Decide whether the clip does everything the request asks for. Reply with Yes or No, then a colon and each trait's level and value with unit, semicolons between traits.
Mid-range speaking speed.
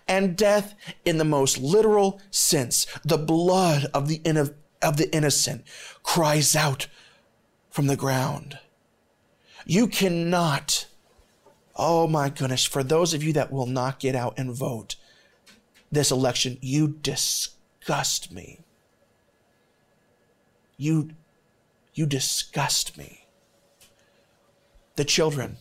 No: slow, 110 wpm